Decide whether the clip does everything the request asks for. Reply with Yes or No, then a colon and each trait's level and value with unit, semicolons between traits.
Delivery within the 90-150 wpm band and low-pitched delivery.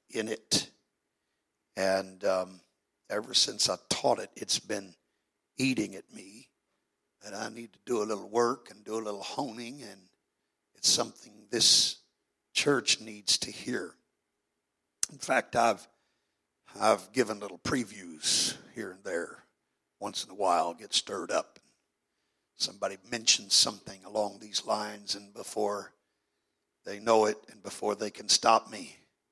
Yes: average, 145 wpm; low, 105 Hz